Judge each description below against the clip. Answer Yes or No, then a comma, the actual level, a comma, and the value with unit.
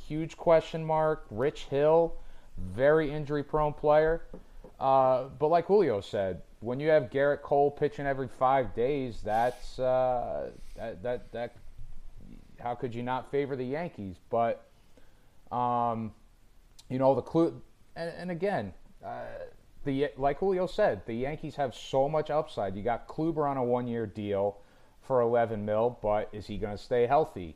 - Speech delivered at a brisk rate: No, average, 155 wpm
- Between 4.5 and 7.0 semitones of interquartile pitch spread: Yes, average, 4.9 semitones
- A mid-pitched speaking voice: No, low, 130 Hz